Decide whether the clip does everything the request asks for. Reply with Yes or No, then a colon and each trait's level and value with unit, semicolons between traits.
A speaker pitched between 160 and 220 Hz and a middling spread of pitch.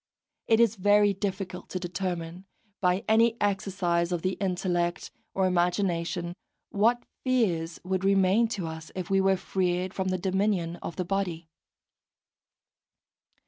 No: medium, 185 Hz; narrow, 2.2 semitones